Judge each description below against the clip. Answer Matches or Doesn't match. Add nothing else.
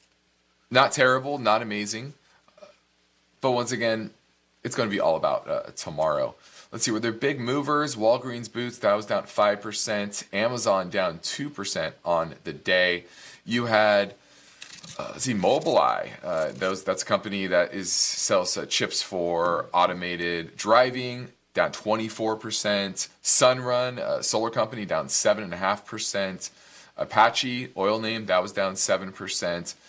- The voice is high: Doesn't match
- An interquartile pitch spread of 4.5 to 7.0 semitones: Matches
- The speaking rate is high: Doesn't match